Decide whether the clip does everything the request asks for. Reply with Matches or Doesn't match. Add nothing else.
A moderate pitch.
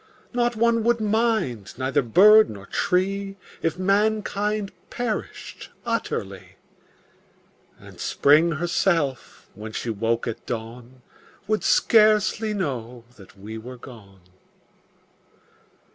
Matches